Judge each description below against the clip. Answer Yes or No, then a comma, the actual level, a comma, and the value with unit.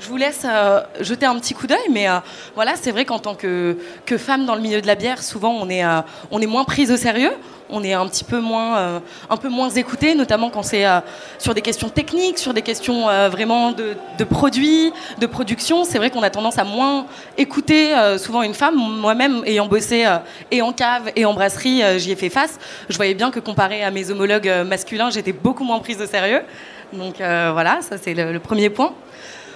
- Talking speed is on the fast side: Yes, fast, 235 wpm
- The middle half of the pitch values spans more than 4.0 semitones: Yes, average, 4.4 semitones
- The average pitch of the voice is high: Yes, high, 225 Hz